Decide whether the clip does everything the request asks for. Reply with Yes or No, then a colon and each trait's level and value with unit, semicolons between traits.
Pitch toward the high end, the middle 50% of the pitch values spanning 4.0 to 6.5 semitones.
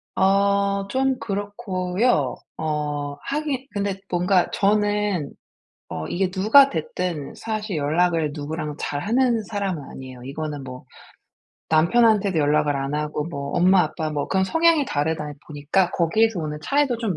No: medium, 180 Hz; wide, 5.6 semitones